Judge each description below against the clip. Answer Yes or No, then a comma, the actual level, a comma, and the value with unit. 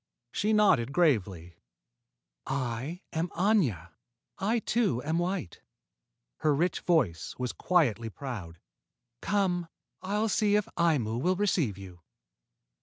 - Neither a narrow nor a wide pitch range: No, wide, 8.7 semitones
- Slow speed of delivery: Yes, slow, 110 wpm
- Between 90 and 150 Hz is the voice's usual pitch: No, medium, 160 Hz